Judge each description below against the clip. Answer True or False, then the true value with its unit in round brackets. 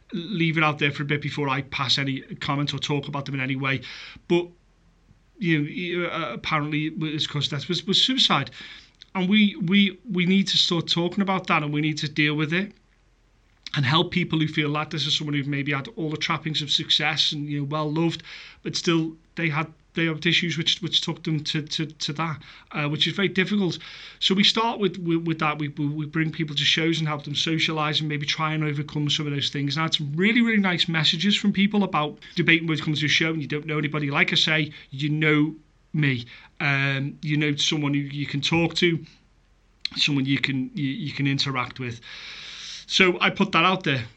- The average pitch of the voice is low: False (155 Hz)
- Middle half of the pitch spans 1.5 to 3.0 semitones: True (2.6 semitones)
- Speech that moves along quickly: True (220 wpm)